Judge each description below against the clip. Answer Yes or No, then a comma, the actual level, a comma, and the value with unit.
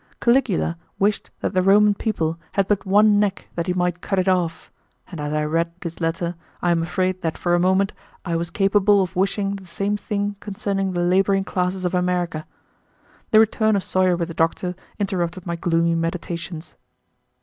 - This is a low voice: No, medium, 185 Hz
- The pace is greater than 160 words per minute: Yes, average, 185 wpm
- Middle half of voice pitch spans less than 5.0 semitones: Yes, average, 2.7 semitones